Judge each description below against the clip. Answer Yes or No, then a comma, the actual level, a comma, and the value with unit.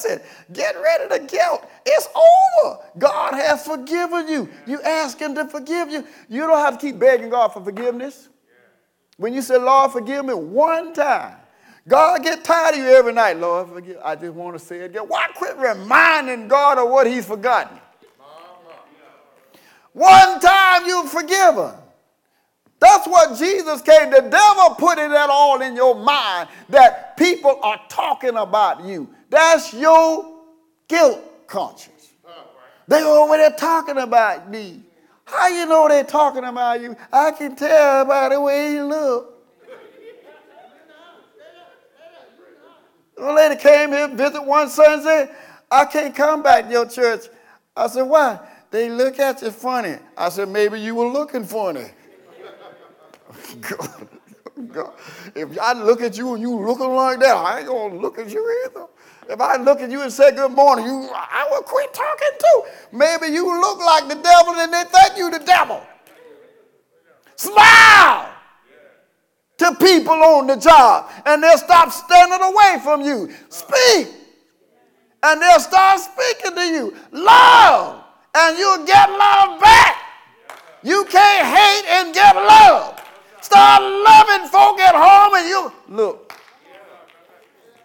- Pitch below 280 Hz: No, very high, 310 Hz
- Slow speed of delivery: No, average, 150 wpm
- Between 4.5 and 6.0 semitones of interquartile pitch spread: Yes, wide, 5.4 semitones